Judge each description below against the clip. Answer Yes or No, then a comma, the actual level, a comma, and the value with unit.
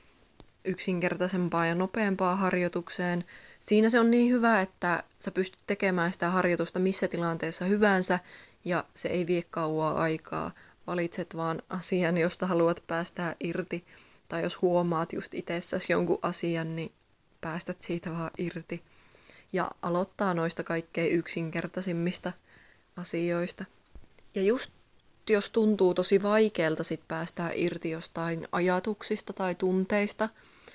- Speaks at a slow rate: No, average, 120 wpm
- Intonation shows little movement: Yes, narrow, 2.0 semitones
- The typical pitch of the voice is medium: Yes, medium, 180 Hz